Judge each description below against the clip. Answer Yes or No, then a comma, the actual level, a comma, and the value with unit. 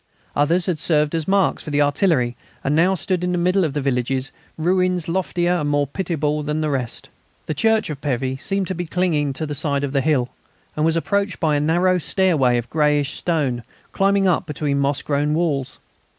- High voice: No, medium, 155 Hz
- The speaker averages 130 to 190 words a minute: No, fast, 205 wpm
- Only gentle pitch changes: No, average, 4.0 semitones